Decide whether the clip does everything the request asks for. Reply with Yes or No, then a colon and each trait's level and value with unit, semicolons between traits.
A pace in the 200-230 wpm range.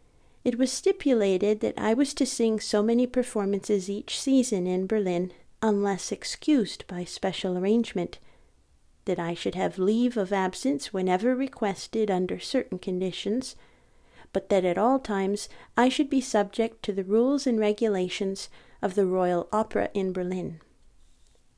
No: average, 145 wpm